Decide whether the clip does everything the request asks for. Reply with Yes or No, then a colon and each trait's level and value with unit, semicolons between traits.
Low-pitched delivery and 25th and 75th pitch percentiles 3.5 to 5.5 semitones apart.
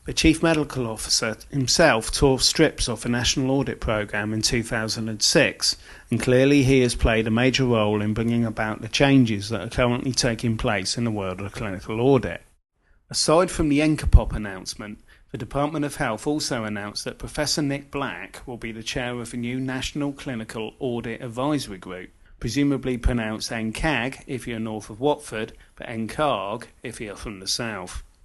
Yes: low, 120 Hz; average, 3.8 semitones